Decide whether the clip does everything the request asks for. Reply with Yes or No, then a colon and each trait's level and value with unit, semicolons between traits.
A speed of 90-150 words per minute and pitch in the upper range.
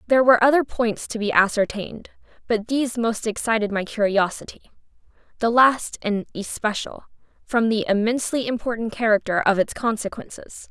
Yes: slow, 135 wpm; high, 225 Hz